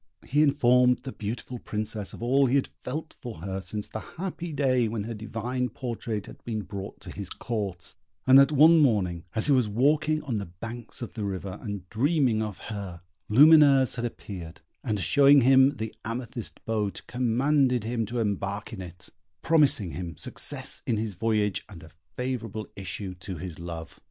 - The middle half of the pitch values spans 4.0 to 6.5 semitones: Yes, average, 4.6 semitones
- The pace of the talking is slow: No, average, 180 wpm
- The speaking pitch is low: Yes, low, 115 Hz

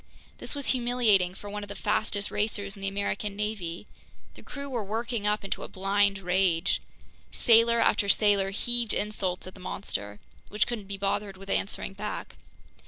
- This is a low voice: No, high, 200 Hz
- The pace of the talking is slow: No, average, 170 wpm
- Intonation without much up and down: Yes, narrow, 1.9 semitones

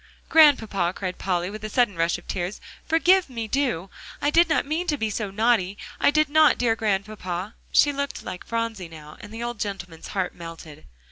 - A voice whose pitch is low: No, high, 215 Hz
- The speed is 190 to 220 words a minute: Yes, average, 195 wpm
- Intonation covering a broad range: Yes, wide, 7.1 semitones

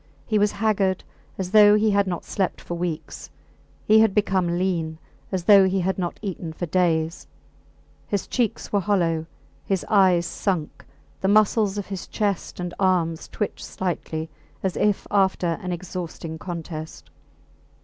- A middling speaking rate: Yes, average, 150 wpm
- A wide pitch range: No, average, 2.8 semitones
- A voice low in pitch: No, medium, 185 Hz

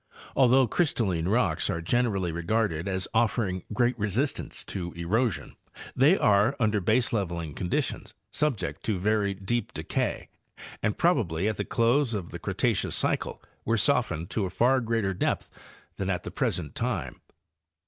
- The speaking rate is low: No, average, 145 wpm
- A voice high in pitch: No, low, 105 Hz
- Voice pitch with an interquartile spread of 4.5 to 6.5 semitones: Yes, average, 4.8 semitones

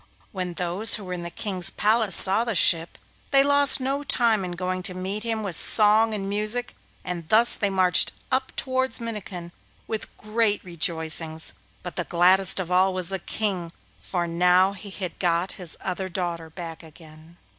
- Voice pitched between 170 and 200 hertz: Yes, medium, 185 Hz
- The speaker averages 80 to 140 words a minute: No, average, 175 wpm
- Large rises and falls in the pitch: No, average, 3.7 semitones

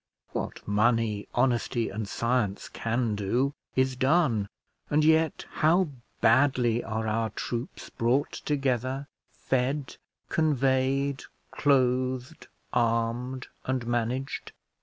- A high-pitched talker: No, low, 125 Hz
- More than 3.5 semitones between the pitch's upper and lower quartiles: No, average, 2.9 semitones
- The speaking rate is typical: No, slow, 95 wpm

